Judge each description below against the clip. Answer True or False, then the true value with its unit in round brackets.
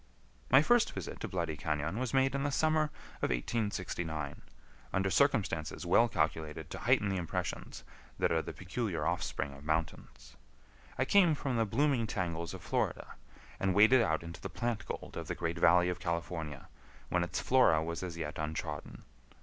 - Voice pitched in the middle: False (90 Hz)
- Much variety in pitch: True (7.0 semitones)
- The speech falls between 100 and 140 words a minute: False (175 wpm)